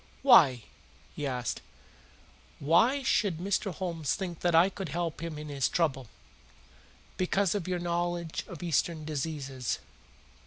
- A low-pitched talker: No, medium, 170 Hz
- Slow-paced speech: Yes, slow, 130 wpm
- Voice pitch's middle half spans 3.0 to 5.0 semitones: Yes, average, 3.4 semitones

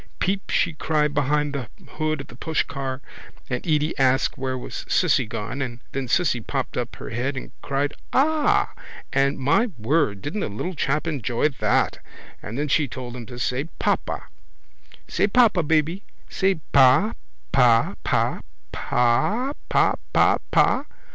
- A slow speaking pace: No, average, 155 wpm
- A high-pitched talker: No, medium, 140 Hz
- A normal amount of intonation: Yes, average, 4.1 semitones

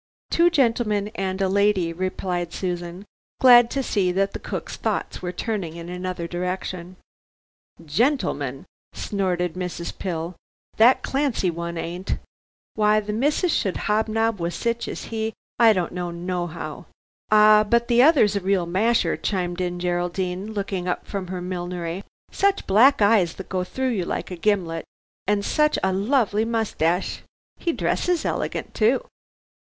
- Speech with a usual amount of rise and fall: Yes, average, 4.0 semitones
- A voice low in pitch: No, high, 190 Hz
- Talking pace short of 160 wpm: Yes, average, 150 wpm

